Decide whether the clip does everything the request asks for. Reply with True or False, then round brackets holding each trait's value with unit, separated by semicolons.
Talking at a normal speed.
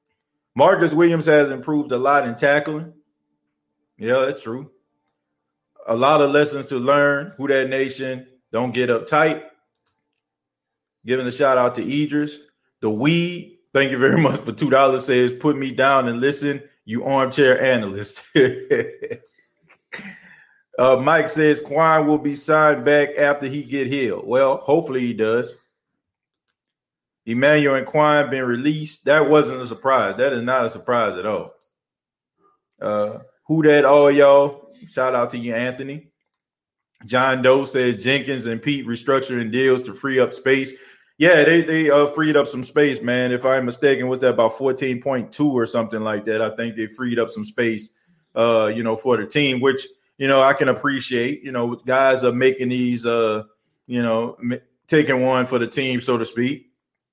True (170 wpm)